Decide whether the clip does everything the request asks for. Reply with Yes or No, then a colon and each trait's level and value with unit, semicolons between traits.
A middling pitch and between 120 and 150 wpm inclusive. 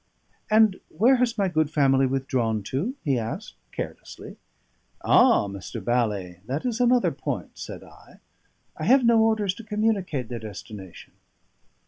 Yes: medium, 150 Hz; average, 140 wpm